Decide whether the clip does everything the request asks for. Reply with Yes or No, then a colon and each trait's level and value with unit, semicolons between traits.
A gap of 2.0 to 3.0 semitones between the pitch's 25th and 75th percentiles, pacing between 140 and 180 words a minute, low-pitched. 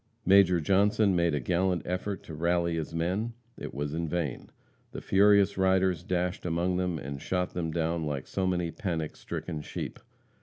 Yes: narrow, 2.4 semitones; average, 165 wpm; very low, 90 Hz